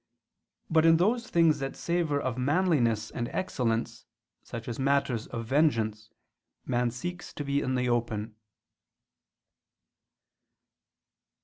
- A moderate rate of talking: No, slow, 115 wpm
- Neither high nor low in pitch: No, low, 130 Hz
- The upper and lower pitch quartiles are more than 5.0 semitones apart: Yes, wide, 5.4 semitones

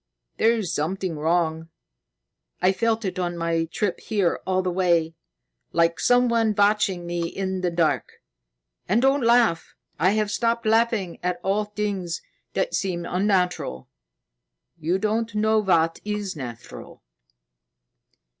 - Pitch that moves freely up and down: No, average, 4.0 semitones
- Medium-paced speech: No, slow, 125 wpm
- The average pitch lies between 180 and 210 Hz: Yes, high, 190 Hz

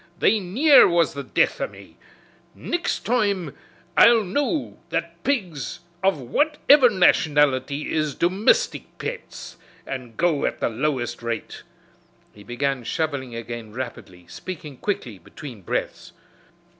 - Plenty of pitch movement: Yes, wide, 8.3 semitones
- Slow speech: Yes, slow, 120 wpm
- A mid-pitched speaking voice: Yes, medium, 155 Hz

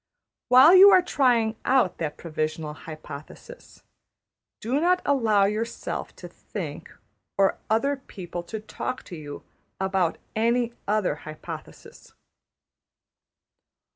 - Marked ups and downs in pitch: Yes, wide, 7.1 semitones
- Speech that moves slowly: Yes, slow, 105 wpm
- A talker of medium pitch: No, high, 220 Hz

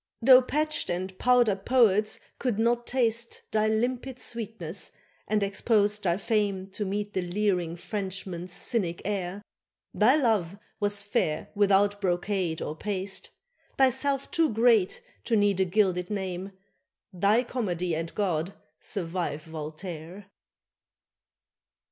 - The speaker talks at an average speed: No, slow, 120 wpm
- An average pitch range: Yes, average, 3.7 semitones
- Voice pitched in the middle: No, high, 200 Hz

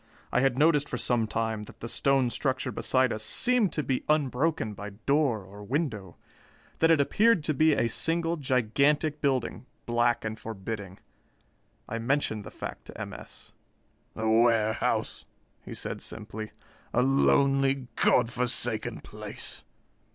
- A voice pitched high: No, low, 125 Hz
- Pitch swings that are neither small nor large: Yes, average, 4.5 semitones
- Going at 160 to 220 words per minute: No, average, 145 wpm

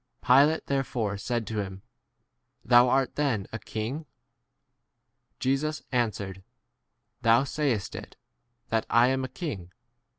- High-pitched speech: No, low, 120 Hz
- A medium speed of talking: No, slow, 120 wpm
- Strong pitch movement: No, average, 3.9 semitones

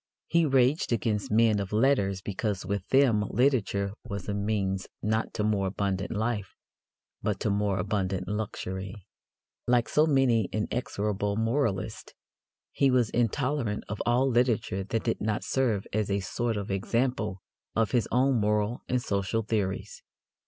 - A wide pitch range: No, average, 3.3 semitones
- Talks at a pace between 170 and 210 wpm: No, average, 145 wpm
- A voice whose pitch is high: No, low, 105 Hz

